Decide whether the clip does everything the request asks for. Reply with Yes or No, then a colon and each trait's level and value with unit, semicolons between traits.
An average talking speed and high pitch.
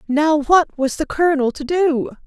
Yes: average, 185 wpm; very high, 295 Hz